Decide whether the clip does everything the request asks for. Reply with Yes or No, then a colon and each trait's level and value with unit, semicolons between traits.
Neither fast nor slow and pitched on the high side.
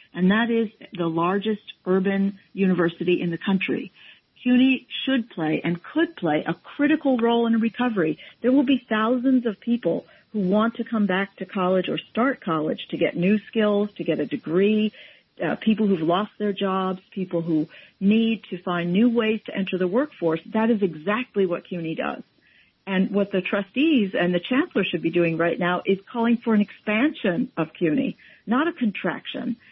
Yes: average, 185 wpm; high, 200 Hz